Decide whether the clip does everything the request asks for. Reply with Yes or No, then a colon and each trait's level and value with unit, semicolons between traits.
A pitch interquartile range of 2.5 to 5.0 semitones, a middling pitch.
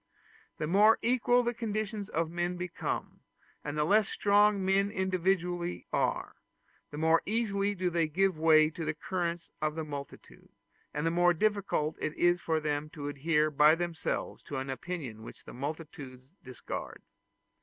Yes: average, 4.2 semitones; medium, 170 Hz